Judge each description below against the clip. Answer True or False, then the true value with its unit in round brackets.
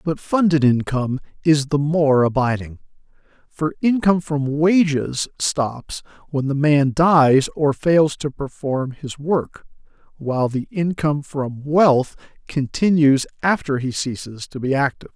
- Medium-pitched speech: True (145 Hz)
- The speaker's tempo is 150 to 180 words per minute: False (135 wpm)